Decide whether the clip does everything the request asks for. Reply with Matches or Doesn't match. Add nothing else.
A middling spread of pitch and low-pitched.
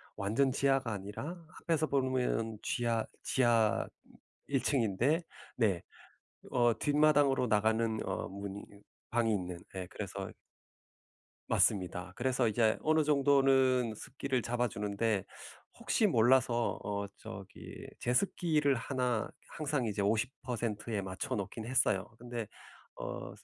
Matches